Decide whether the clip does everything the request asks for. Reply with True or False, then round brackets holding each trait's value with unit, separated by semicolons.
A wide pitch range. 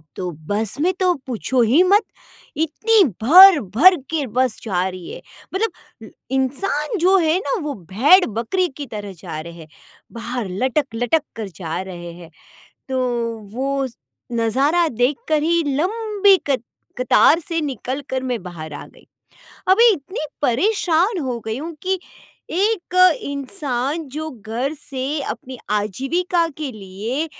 True (7.3 semitones)